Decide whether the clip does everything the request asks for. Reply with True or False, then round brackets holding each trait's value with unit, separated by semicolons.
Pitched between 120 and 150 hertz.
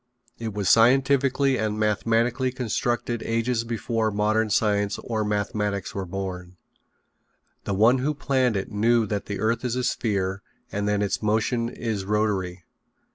False (110 Hz)